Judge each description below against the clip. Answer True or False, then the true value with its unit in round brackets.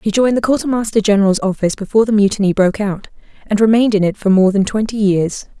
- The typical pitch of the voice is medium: False (205 Hz)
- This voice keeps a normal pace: False (215 wpm)